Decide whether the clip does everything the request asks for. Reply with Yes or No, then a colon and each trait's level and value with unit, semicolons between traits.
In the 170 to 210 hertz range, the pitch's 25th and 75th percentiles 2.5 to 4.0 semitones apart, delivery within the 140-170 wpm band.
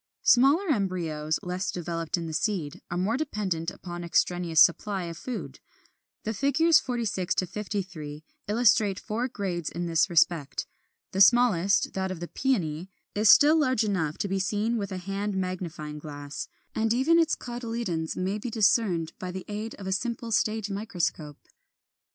No: high, 190 Hz; average, 4.6 semitones; average, 165 wpm